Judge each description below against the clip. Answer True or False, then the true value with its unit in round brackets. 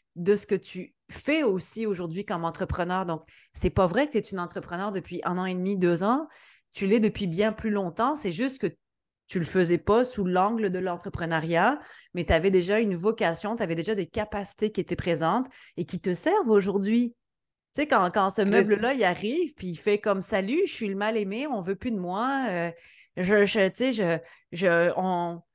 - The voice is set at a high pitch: True (195 Hz)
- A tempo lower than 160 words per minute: False (205 wpm)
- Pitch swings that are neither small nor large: True (3.3 semitones)